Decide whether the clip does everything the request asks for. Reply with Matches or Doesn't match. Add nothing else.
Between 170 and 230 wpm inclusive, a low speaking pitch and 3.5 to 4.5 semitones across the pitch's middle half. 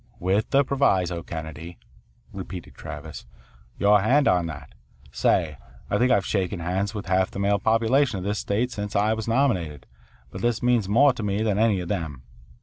Matches